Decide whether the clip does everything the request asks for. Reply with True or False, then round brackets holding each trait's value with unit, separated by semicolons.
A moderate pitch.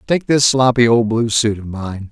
False (115 Hz)